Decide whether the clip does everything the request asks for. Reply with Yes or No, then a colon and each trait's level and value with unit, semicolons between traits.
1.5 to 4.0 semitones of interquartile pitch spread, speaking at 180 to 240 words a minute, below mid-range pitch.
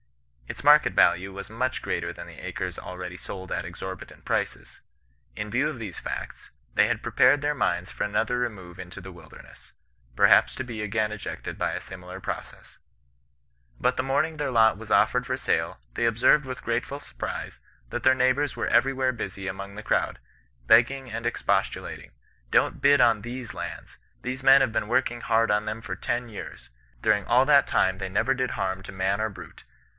No: average, 4.9 semitones; average, 190 wpm; low, 115 Hz